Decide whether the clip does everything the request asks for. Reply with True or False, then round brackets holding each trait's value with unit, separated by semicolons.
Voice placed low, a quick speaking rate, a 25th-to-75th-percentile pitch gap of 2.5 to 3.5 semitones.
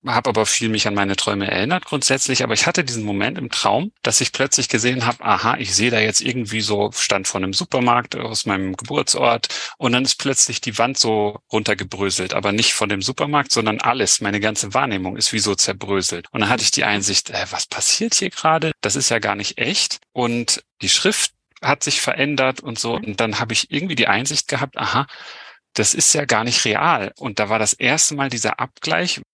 False (110 Hz; 215 wpm; 4.1 semitones)